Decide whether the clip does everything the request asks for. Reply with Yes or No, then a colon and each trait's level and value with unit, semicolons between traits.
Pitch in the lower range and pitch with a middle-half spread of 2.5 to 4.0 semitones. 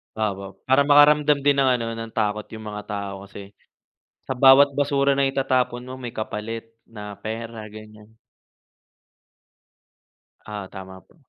No: low, 115 Hz; average, 4.4 semitones